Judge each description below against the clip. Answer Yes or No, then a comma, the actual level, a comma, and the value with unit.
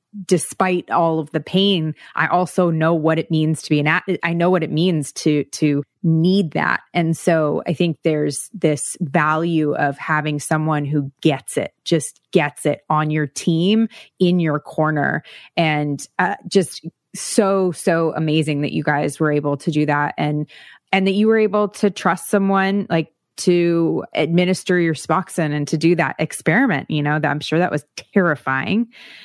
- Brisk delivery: No, average, 175 wpm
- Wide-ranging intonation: No, average, 3.1 semitones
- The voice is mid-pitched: Yes, medium, 160 Hz